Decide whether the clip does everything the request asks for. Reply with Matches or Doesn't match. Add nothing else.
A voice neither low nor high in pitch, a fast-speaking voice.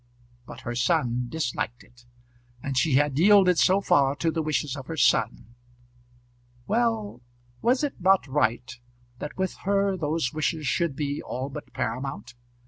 Doesn't match